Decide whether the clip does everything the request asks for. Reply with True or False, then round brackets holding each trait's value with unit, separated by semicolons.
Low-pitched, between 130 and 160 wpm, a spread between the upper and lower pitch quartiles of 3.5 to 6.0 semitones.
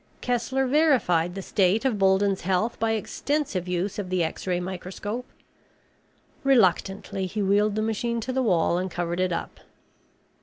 False (195 Hz; 155 wpm; 4.1 semitones)